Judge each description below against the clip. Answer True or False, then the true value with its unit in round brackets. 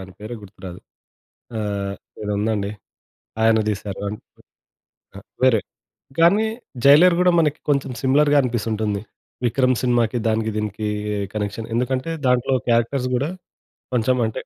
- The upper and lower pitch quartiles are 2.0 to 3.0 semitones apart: False (3.8 semitones)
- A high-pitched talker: False (115 Hz)